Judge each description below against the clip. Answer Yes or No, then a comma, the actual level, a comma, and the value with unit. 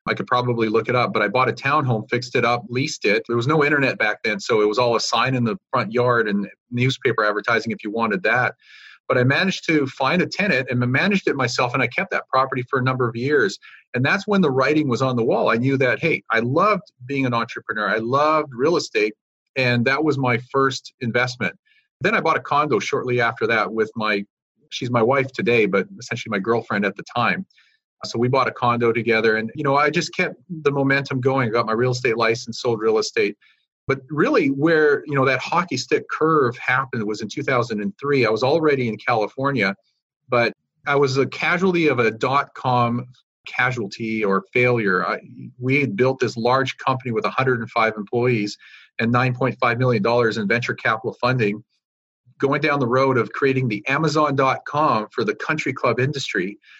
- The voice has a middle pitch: No, low, 130 Hz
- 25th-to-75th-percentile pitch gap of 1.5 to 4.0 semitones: Yes, average, 3.2 semitones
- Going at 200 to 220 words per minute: Yes, fast, 205 wpm